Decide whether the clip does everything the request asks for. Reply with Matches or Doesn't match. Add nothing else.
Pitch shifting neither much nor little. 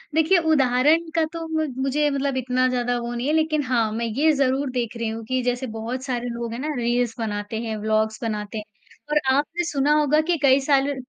Matches